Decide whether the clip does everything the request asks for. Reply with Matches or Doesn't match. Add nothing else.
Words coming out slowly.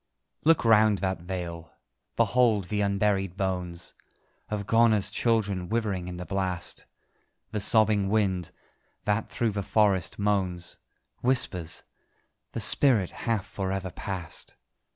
Matches